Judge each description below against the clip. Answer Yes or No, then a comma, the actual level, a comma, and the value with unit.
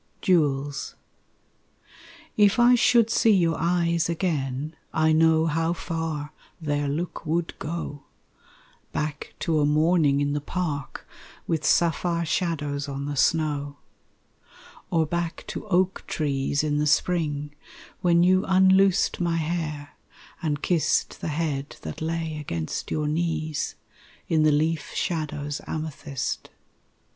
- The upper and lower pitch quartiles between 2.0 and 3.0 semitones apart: Yes, average, 2.7 semitones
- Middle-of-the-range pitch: Yes, medium, 160 Hz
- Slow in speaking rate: Yes, slow, 125 wpm